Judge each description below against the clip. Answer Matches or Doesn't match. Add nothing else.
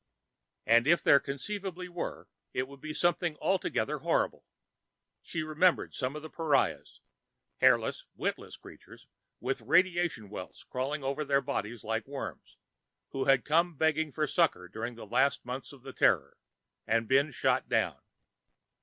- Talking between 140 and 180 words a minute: Matches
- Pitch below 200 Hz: Matches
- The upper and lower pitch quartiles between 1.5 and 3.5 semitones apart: Doesn't match